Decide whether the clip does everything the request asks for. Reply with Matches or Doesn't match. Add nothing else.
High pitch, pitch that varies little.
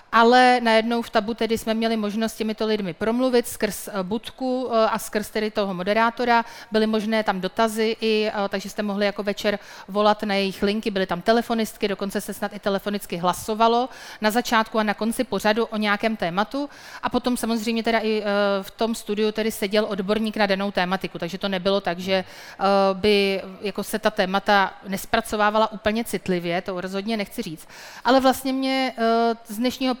Matches